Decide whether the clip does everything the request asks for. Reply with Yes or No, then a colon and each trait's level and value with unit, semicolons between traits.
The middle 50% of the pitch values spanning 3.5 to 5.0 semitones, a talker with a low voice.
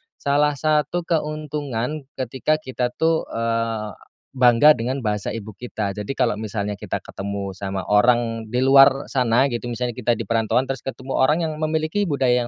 Yes: average, 4.5 semitones; low, 125 Hz